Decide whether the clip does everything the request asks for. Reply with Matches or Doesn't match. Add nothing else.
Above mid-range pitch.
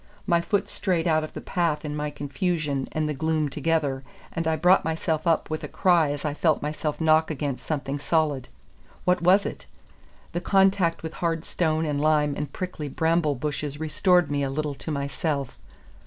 Doesn't match